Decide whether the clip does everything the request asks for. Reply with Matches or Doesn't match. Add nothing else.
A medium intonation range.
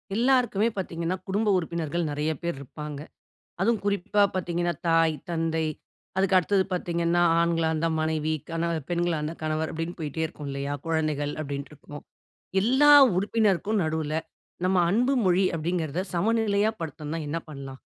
Matches